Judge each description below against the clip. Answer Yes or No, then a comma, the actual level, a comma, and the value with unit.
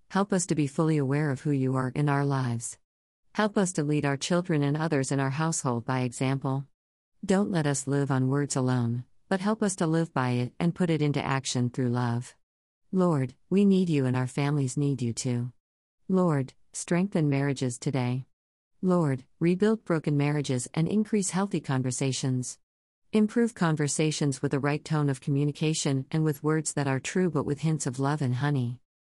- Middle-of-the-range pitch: Yes, medium, 145 Hz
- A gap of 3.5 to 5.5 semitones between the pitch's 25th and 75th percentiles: Yes, average, 3.9 semitones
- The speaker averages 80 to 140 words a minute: No, average, 185 wpm